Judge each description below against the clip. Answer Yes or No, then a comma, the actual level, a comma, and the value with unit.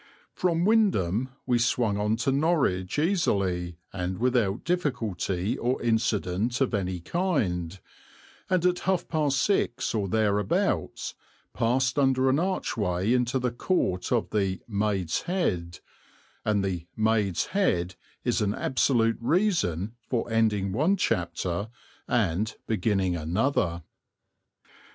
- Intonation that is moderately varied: No, wide, 6.2 semitones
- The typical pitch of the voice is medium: No, low, 110 Hz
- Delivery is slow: Yes, slow, 120 wpm